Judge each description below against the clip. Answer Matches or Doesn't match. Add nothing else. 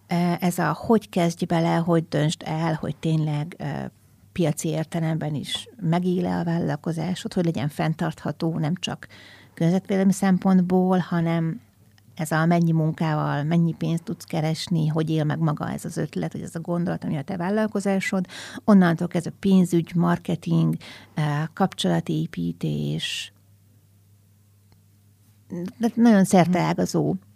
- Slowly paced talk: Doesn't match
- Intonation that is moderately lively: Matches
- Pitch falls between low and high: Matches